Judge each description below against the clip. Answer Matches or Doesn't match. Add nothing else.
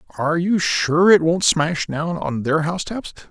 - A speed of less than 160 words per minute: Doesn't match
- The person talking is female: Doesn't match